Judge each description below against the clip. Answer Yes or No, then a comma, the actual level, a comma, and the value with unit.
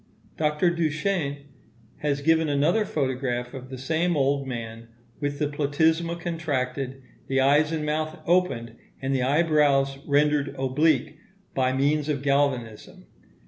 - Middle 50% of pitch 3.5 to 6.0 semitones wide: No, average, 2.8 semitones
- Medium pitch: Yes, medium, 145 Hz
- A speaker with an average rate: No, slow, 130 wpm